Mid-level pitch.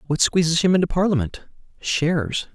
Yes: medium, 160 Hz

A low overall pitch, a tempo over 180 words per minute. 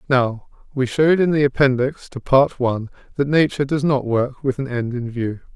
Yes: low, 130 Hz; fast, 205 wpm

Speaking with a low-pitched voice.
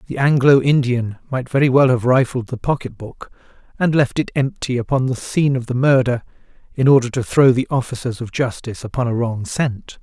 Yes: low, 125 Hz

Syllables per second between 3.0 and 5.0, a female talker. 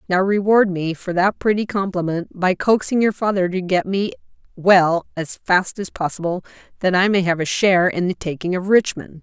No: 5.2 syllables/s; female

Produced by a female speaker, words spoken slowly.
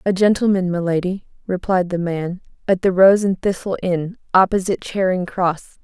No: female; average, 165 wpm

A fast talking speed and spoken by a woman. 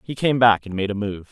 No: fast, 320 wpm; male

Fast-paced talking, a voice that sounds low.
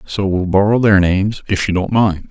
Yes: fast, 235 wpm; low, 100 Hz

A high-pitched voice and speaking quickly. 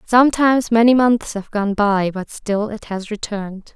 No: high, 215 Hz; average, 175 wpm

